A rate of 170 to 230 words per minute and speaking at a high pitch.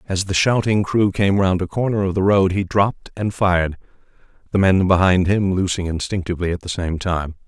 No: average, 200 wpm; very low, 95 Hz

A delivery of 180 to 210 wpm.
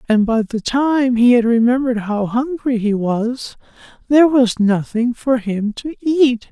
No: average, 165 wpm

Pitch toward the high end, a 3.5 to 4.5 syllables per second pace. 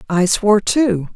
Yes: high, 205 Hz; 4.4 syllables/s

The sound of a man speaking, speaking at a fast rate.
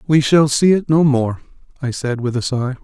Yes: male; fast, 235 wpm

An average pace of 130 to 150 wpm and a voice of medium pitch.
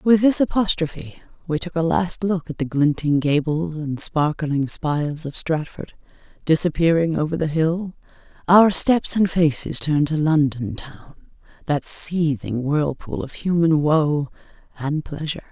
Yes: average, 145 wpm; medium, 155 Hz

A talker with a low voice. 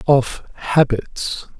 Yes: low, 130 Hz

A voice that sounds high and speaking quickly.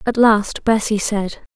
No: high, 215 Hz; average, 155 wpm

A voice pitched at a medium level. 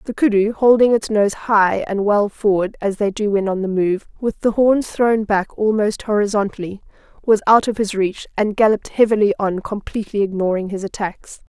No: high, 205 Hz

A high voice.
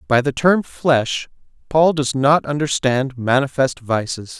No: low, 135 Hz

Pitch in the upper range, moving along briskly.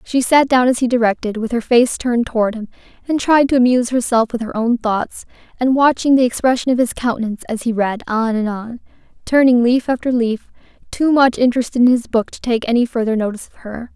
Yes: high, 240 Hz; fast, 220 wpm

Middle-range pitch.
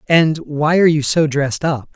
Yes: medium, 150 Hz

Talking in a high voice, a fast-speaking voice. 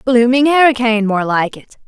No: high, 235 Hz; average, 160 wpm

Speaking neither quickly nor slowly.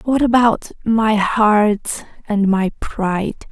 No: slow, 120 wpm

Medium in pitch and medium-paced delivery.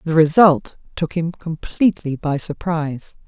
No: medium, 160 Hz; slow, 130 wpm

